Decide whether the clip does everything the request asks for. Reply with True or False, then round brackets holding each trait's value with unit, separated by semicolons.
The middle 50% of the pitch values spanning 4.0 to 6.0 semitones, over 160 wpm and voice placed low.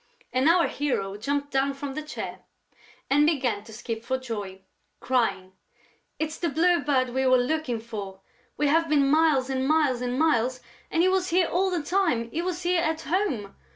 False (4.8 semitones; 190 wpm; 275 Hz)